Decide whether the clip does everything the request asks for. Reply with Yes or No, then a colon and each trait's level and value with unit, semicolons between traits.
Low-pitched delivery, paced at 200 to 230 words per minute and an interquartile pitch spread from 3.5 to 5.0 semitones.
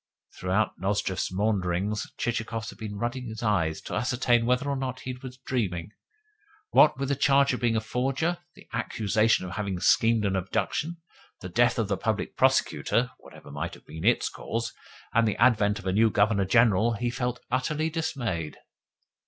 No: low, 115 Hz; average, 175 wpm; average, 3.9 semitones